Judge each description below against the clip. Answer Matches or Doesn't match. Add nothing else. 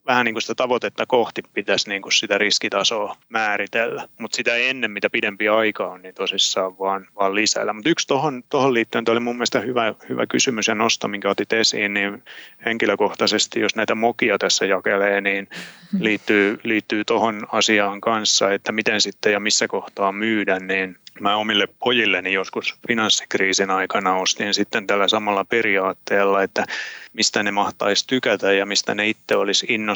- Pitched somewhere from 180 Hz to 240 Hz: Doesn't match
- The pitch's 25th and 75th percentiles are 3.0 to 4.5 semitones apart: Doesn't match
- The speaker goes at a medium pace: Doesn't match